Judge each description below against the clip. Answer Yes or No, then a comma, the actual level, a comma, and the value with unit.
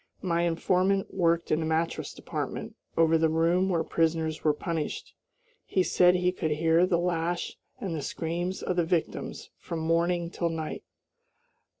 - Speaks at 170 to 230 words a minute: No, average, 160 wpm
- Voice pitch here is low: No, medium, 170 Hz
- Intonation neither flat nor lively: No, narrow, 1.7 semitones